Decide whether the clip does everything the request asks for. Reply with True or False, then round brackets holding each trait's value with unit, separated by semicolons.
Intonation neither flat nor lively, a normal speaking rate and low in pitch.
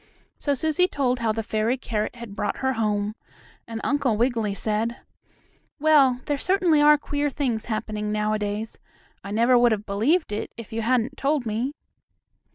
False (4.4 semitones; 165 wpm; 235 Hz)